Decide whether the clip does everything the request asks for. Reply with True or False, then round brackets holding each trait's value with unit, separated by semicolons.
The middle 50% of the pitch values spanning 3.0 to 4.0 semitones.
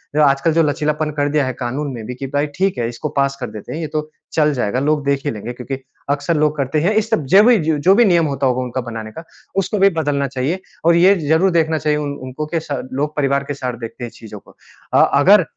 True (3.5 semitones)